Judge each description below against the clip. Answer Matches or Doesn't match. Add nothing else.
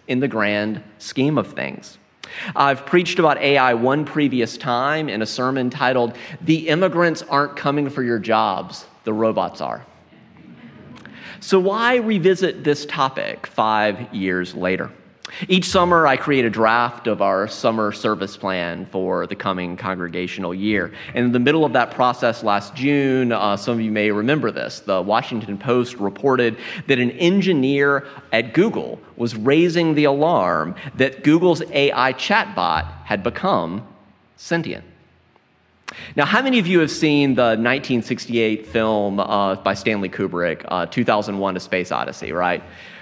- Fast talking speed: Doesn't match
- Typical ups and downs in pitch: Doesn't match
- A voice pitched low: Matches